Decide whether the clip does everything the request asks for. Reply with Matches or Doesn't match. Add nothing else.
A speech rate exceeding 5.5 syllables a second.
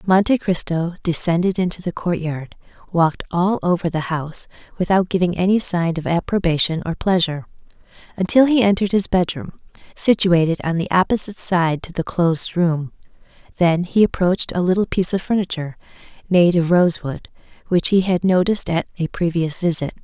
Matches